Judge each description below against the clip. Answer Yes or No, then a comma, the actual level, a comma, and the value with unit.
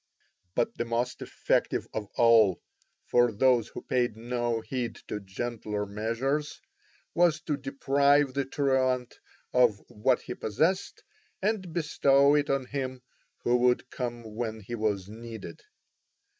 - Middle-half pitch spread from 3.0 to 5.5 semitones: Yes, average, 3.5 semitones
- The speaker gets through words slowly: Yes, slow, 130 wpm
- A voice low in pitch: Yes, low, 125 Hz